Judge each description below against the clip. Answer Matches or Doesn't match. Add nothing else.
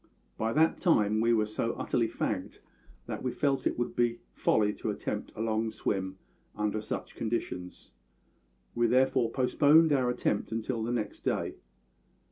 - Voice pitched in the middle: Doesn't match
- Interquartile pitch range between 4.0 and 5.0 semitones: Doesn't match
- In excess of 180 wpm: Doesn't match